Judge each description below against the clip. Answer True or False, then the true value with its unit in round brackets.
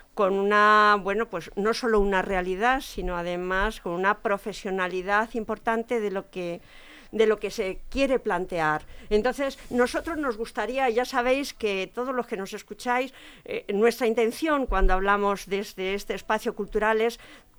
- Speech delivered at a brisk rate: False (160 wpm)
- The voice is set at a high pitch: True (215 Hz)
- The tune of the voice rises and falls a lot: False (3.6 semitones)